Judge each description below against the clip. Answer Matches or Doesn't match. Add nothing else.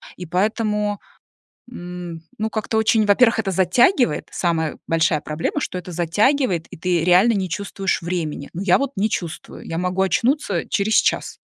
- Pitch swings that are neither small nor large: Matches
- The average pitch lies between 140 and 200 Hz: Matches